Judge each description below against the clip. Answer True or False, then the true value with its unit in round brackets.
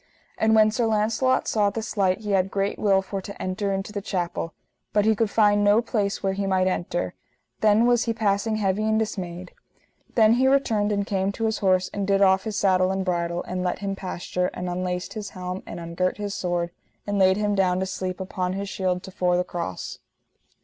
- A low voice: False (195 Hz)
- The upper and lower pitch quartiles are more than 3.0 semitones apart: False (2.4 semitones)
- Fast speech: True (215 wpm)